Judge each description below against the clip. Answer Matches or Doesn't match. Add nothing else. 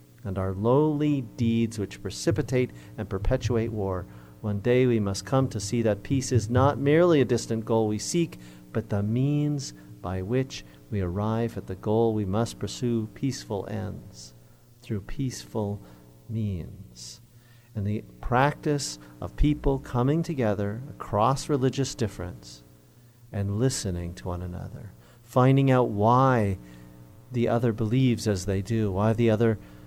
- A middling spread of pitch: Matches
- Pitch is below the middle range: Matches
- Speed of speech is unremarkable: Matches